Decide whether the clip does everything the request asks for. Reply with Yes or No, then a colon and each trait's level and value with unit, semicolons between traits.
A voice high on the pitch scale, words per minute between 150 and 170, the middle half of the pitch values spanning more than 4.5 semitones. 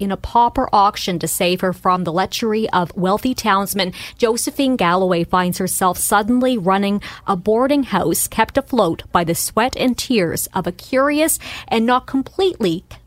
Yes: high, 200 Hz; average, 160 wpm; average, 5.3 semitones